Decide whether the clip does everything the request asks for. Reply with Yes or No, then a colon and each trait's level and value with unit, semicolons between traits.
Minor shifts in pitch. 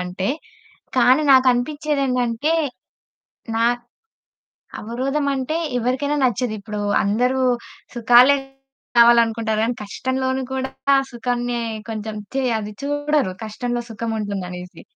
No: average, 3.1 semitones